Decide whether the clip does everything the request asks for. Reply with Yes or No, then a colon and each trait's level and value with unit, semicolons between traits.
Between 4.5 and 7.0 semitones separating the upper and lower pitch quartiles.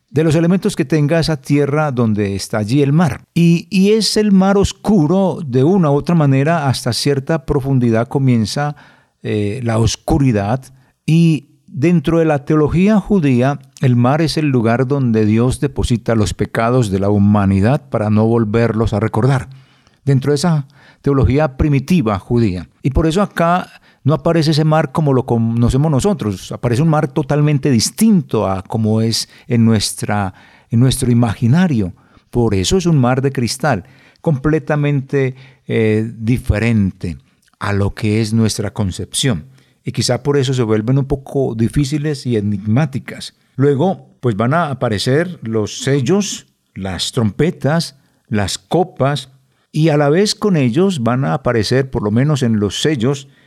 Yes: wide, 5.4 semitones